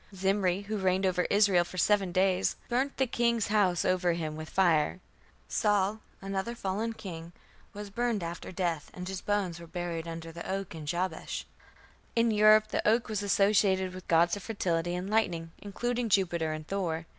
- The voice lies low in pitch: No, high, 190 Hz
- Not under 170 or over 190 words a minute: Yes, average, 175 wpm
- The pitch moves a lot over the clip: No, average, 3.2 semitones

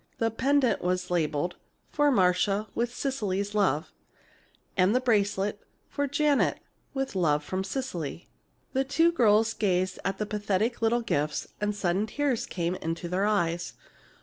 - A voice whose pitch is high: Yes, high, 205 Hz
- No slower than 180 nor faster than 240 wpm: No, average, 145 wpm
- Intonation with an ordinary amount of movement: Yes, average, 4.9 semitones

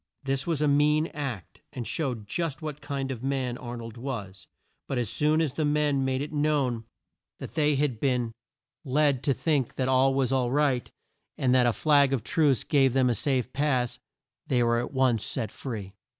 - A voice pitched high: No, low, 135 Hz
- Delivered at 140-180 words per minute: No, average, 195 wpm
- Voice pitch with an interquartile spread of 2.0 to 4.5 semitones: Yes, average, 3.0 semitones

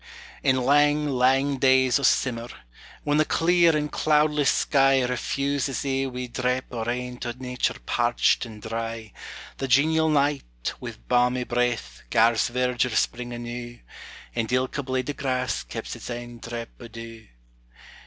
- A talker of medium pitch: No, low, 125 Hz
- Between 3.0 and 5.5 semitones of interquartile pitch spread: No, narrow, 2.6 semitones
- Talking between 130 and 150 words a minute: Yes, average, 145 wpm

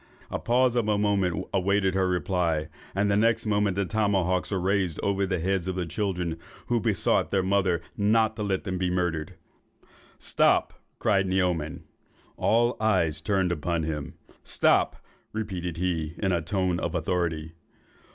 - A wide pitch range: No, average, 2.8 semitones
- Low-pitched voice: Yes, very low, 95 Hz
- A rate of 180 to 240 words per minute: No, average, 160 wpm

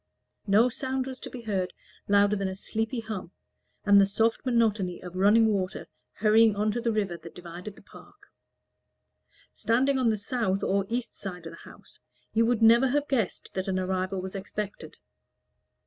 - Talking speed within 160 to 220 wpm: Yes, average, 180 wpm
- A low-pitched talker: No, high, 210 Hz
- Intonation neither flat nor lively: Yes, average, 3.3 semitones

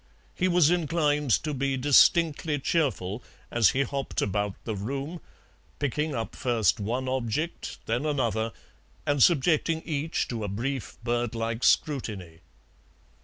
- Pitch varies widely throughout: No, average, 4.9 semitones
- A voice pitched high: No, low, 135 Hz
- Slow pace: Yes, slow, 130 wpm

